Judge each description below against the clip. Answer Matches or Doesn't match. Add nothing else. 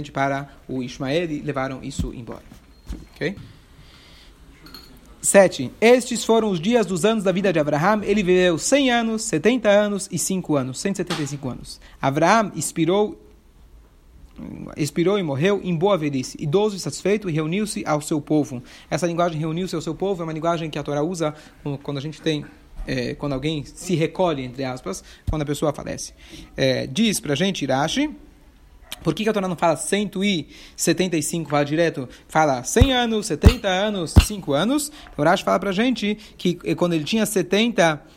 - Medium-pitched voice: Matches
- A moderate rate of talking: Matches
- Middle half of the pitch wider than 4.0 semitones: Matches